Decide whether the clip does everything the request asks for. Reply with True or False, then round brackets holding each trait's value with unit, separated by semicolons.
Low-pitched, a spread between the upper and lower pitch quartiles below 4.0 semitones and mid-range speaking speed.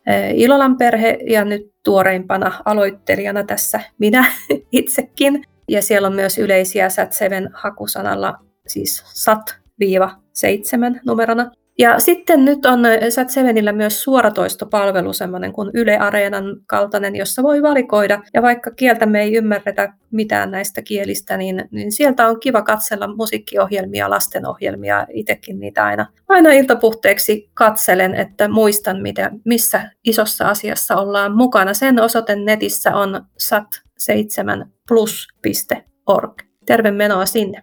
False (210 Hz; 2.9 semitones; 120 wpm)